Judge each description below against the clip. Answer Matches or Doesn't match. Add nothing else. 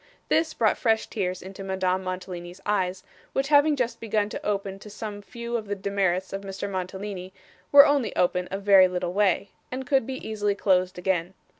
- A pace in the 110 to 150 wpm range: Doesn't match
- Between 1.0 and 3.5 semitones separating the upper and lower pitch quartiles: Matches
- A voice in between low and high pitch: Doesn't match